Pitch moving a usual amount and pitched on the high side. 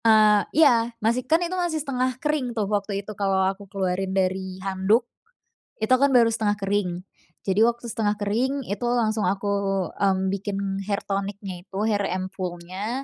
Yes: average, 3.5 semitones; high, 205 Hz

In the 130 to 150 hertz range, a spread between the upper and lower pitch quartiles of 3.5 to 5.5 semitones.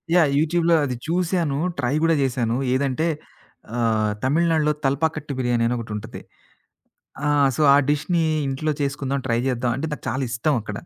Yes: medium, 140 Hz; average, 4.4 semitones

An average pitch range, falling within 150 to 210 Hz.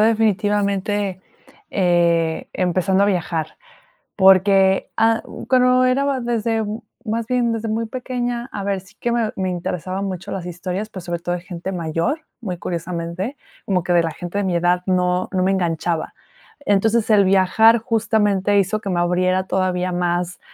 Yes: average, 3.7 semitones; high, 190 Hz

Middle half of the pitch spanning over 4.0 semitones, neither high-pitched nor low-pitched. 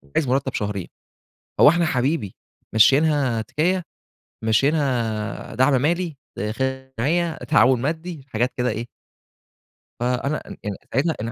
No: average, 4.9 semitones; low, 130 Hz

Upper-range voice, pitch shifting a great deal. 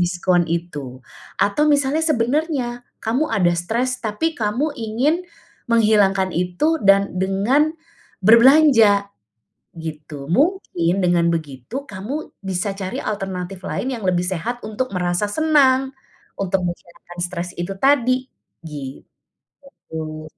Yes: high, 200 Hz; wide, 6.5 semitones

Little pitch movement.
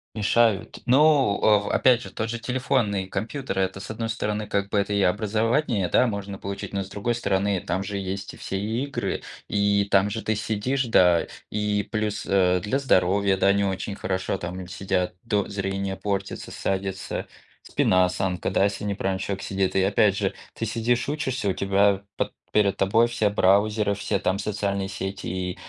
Yes: narrow, 2.1 semitones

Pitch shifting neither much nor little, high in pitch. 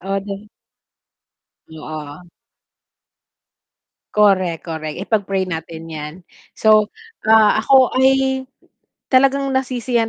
No: wide, 7.2 semitones; high, 205 Hz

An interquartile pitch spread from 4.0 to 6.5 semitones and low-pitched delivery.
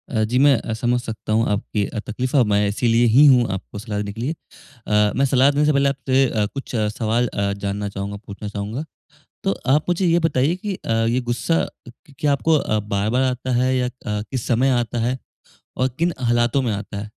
Yes: average, 4.3 semitones; low, 120 Hz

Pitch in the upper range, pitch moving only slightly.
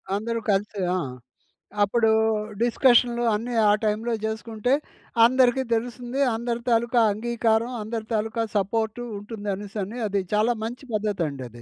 Yes: high, 225 Hz; narrow, 2.3 semitones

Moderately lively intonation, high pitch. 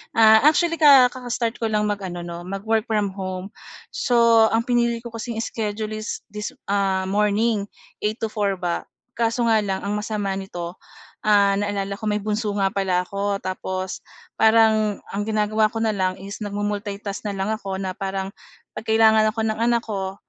No: narrow, 2.2 semitones; high, 210 Hz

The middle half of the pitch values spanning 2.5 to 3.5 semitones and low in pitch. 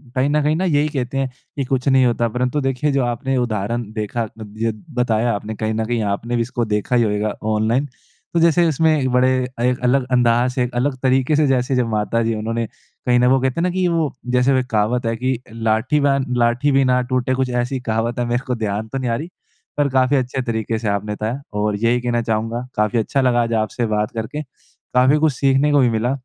Yes: average, 2.8 semitones; low, 125 Hz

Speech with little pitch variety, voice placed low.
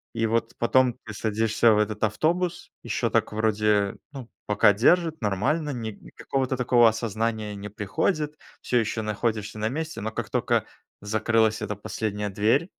No: average, 3.0 semitones; low, 110 Hz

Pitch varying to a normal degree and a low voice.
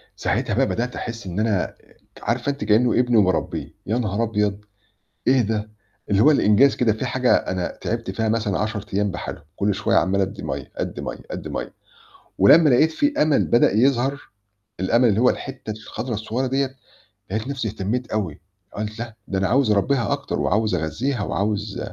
Yes: average, 3.6 semitones; low, 110 Hz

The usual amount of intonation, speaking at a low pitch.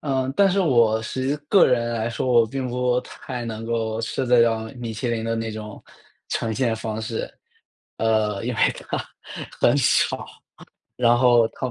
No: narrow, 2.0 semitones; low, 115 Hz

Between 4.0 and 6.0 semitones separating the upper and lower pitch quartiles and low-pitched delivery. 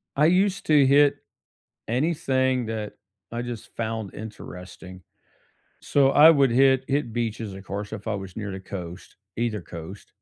Yes: average, 5.2 semitones; low, 115 Hz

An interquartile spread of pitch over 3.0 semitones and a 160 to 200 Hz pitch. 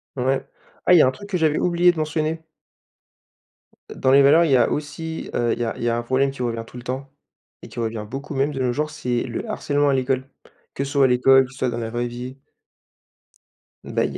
No: average, 3.4 semitones; low, 135 Hz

